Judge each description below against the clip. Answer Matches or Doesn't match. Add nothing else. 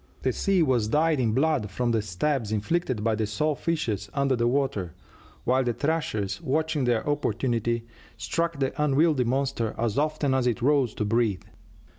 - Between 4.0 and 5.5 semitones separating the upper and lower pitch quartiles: Matches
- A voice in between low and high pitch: Doesn't match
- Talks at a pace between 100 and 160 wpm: Doesn't match